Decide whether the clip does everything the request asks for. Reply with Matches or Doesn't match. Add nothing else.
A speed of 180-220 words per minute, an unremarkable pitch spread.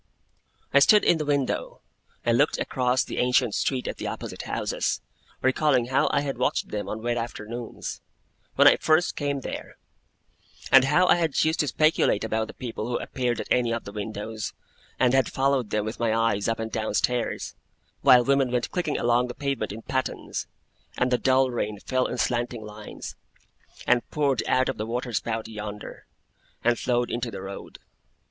Matches